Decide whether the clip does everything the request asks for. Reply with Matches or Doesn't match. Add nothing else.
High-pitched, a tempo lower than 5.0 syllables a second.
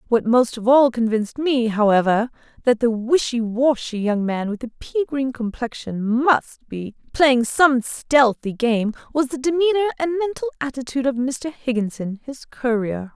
Matches